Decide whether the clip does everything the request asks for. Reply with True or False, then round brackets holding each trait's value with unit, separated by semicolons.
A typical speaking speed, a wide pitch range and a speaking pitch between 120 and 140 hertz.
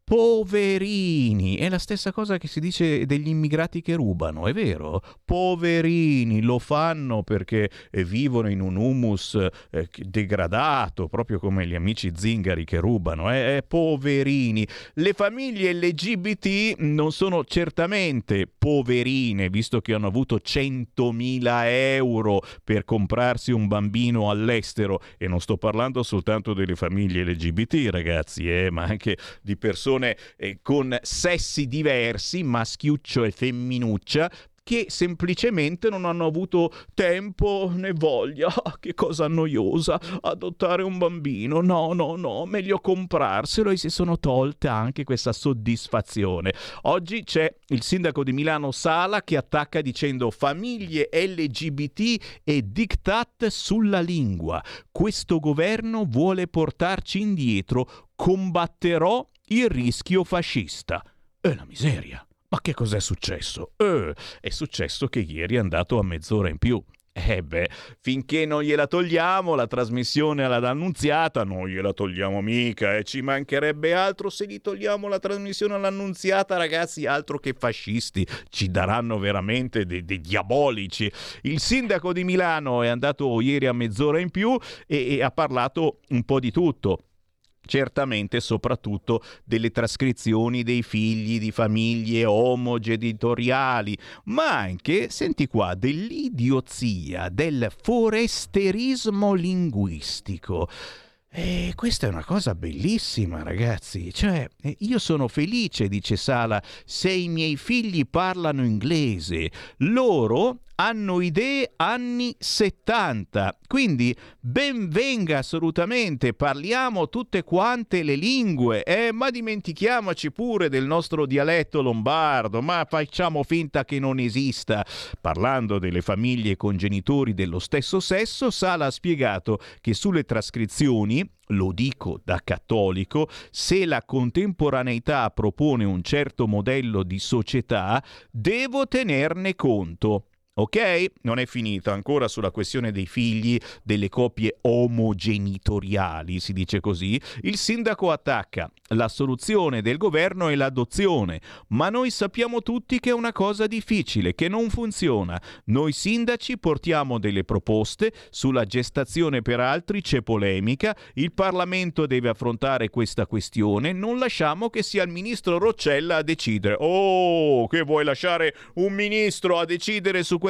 True (125 wpm; 8.5 semitones; 135 Hz)